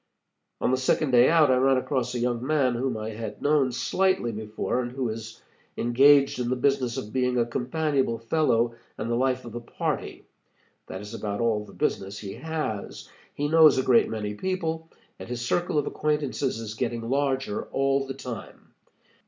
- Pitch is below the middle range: Yes, low, 125 Hz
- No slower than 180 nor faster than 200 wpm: Yes, average, 185 wpm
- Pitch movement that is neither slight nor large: Yes, average, 3.3 semitones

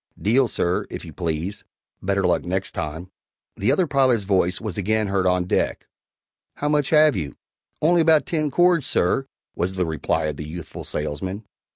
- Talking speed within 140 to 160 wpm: No, average, 175 wpm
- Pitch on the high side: No, low, 100 Hz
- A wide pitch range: Yes, wide, 8.4 semitones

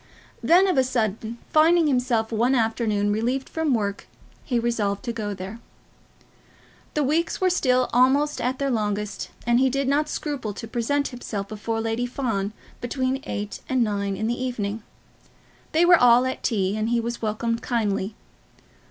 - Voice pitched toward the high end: Yes, high, 235 Hz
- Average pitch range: Yes, average, 3.5 semitones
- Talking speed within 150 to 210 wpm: Yes, average, 165 wpm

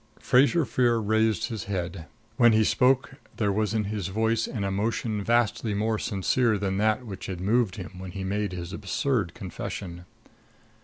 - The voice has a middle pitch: No, low, 105 Hz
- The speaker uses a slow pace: No, average, 165 wpm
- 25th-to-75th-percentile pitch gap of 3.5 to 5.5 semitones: No, average, 2.9 semitones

